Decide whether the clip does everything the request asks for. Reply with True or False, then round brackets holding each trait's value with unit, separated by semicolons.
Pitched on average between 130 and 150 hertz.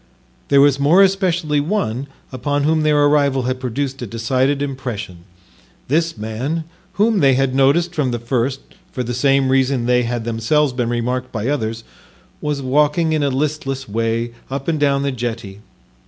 True (135 Hz)